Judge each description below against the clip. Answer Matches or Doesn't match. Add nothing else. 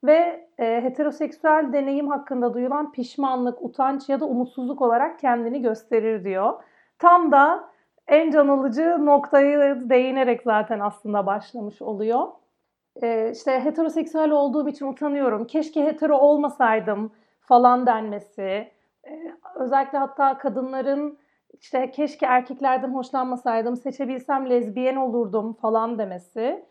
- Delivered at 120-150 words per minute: Doesn't match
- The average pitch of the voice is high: Matches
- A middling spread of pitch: Matches